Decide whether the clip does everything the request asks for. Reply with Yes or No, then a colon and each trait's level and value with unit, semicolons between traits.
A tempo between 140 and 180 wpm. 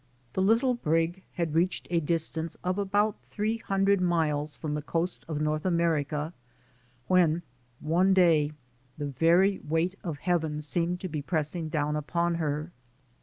Yes: average, 155 wpm